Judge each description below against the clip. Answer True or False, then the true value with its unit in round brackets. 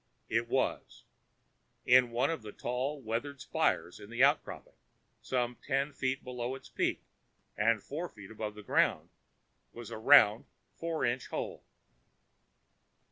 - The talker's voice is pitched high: False (125 Hz)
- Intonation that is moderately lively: True (3.3 semitones)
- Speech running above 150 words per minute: False (135 wpm)